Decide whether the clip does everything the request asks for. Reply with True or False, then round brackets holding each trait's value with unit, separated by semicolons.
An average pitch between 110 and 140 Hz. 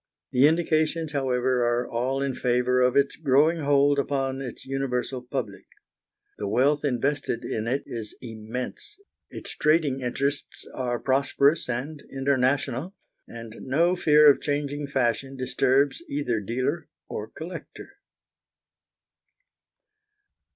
True (135 Hz)